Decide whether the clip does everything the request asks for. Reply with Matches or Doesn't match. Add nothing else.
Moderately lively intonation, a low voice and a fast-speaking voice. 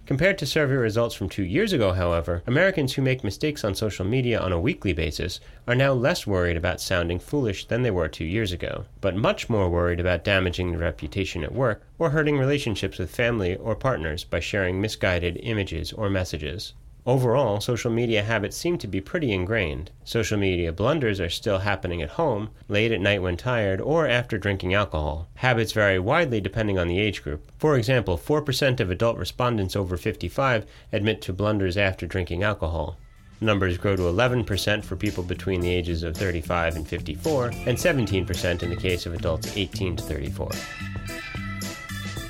Doesn't match